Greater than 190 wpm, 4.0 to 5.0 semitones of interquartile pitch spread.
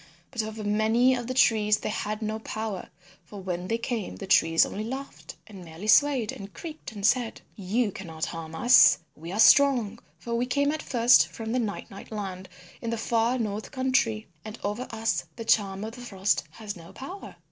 No: average, 200 wpm; average, 3.2 semitones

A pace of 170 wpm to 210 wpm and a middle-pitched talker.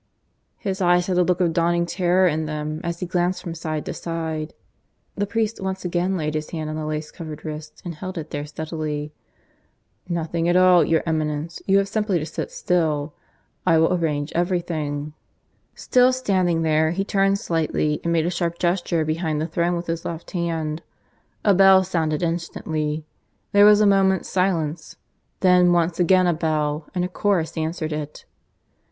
Yes: average, 180 wpm; medium, 170 Hz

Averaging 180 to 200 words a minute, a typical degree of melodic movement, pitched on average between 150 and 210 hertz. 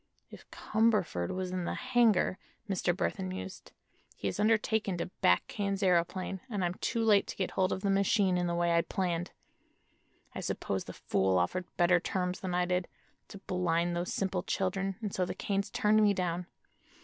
No: average, 185 wpm; narrow, 2.2 semitones; medium, 185 Hz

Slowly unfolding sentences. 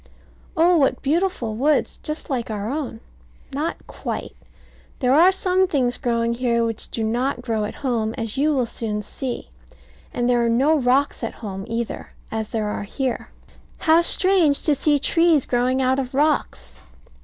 No: average, 165 wpm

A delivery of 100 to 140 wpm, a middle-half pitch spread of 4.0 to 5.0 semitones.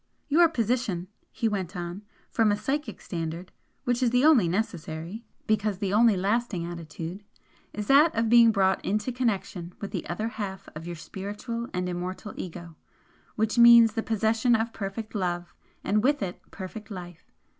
No: average, 165 wpm; average, 4.3 semitones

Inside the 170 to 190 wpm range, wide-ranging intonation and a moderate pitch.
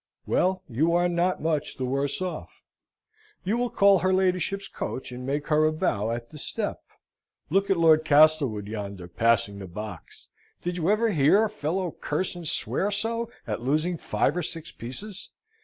Yes: average, 175 wpm; wide, 6.5 semitones; medium, 155 Hz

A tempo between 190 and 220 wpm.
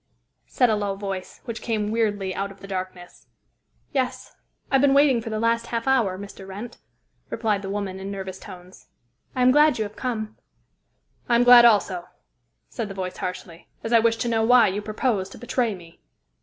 Yes: average, 195 wpm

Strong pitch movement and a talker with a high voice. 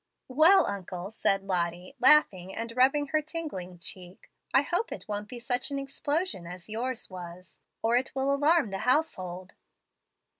Yes: wide, 7.4 semitones; high, 230 Hz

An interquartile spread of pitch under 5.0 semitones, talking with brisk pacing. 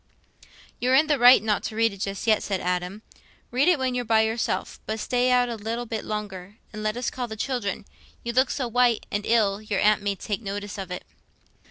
Yes: average, 3.2 semitones; fast, 225 wpm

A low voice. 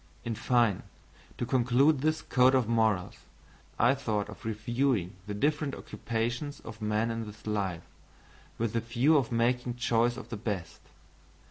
Yes: low, 115 Hz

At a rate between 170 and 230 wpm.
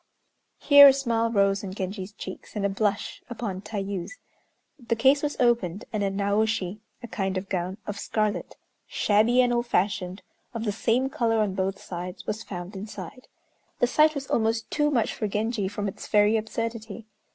Yes: average, 175 wpm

